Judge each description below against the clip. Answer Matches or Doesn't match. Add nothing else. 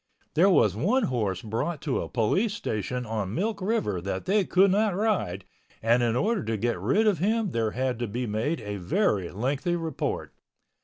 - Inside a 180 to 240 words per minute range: Matches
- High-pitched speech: Doesn't match